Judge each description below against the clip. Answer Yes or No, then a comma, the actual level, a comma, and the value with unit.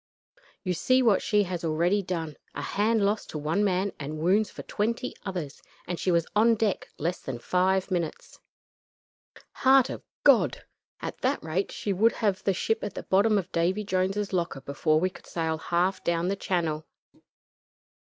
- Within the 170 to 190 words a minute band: Yes, average, 175 wpm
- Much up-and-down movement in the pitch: No, average, 3.7 semitones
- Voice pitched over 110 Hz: Yes, medium, 185 Hz